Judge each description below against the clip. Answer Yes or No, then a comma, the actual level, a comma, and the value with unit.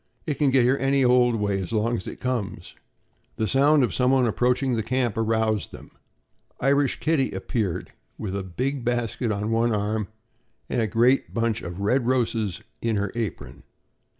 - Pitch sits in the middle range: No, low, 115 Hz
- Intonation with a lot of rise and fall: No, average, 3.3 semitones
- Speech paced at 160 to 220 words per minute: Yes, average, 175 wpm